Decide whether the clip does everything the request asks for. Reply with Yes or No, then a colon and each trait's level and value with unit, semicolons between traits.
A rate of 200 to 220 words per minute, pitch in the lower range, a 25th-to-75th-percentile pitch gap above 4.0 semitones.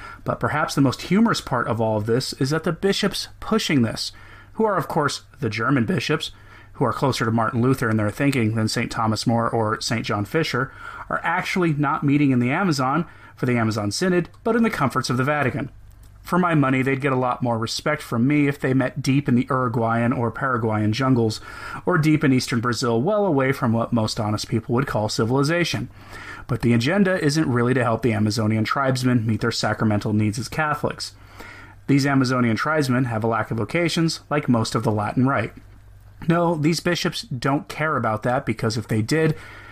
Yes: fast, 205 wpm; low, 125 Hz; average, 4.5 semitones